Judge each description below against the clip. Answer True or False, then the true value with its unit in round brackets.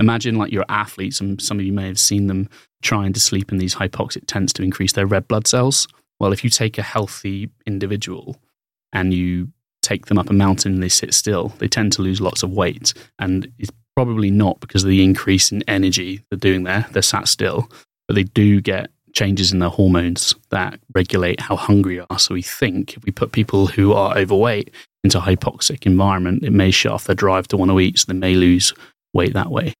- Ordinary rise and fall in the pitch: False (2.3 semitones)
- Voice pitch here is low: True (100 Hz)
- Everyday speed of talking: False (225 wpm)